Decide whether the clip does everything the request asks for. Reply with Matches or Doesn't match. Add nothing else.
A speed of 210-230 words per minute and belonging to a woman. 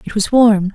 Doesn't match